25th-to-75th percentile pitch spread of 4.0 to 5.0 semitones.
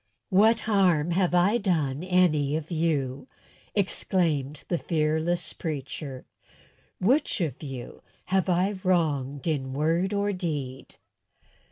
Yes: average, 4.3 semitones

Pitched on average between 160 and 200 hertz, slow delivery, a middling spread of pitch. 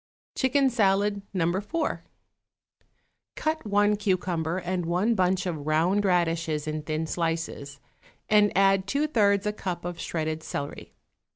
Yes: medium, 185 Hz; slow, 130 wpm; average, 4.0 semitones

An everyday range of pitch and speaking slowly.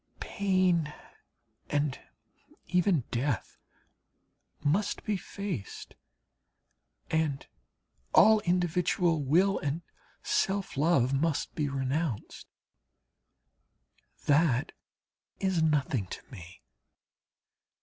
Yes: average, 4.6 semitones; slow, 75 wpm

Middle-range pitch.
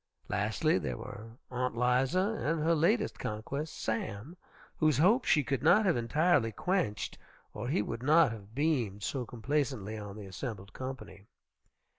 No: low, 130 Hz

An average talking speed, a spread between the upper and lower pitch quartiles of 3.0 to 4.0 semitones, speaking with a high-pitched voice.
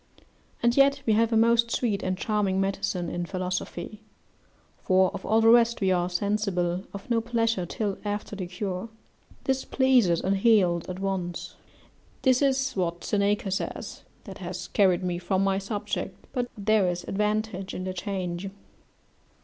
Yes: average, 160 wpm; average, 3.4 semitones; high, 195 Hz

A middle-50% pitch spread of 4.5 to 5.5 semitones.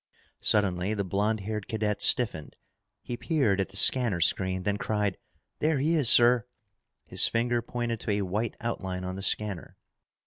No: average, 3.5 semitones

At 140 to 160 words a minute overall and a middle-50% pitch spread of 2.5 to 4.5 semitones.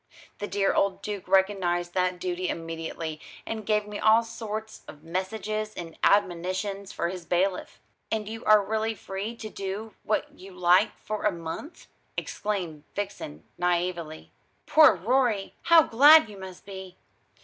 Yes: average, 150 wpm; average, 3.3 semitones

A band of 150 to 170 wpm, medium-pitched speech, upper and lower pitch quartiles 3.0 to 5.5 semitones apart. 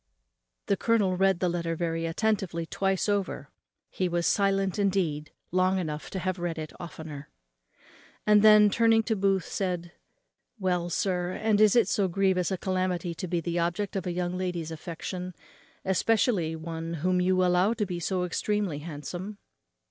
No: average, 165 wpm; medium, 180 Hz; narrow, 2.5 semitones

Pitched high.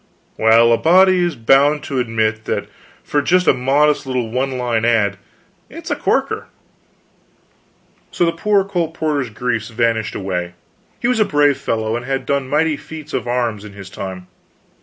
No: low, 125 Hz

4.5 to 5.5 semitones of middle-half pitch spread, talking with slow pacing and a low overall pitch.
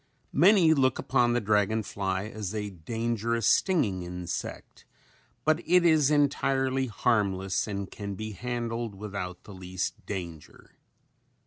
Yes: average, 5.2 semitones; slow, 125 wpm; low, 110 Hz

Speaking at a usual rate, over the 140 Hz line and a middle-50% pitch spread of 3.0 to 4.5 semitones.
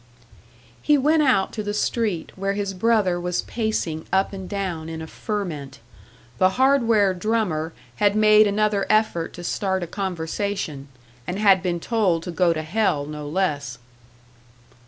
Yes: average, 155 wpm; high, 190 Hz; average, 4.1 semitones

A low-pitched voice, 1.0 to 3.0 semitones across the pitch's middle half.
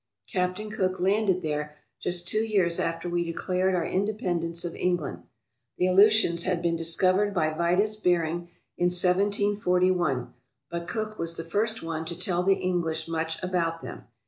No: medium, 180 Hz; narrow, 2.4 semitones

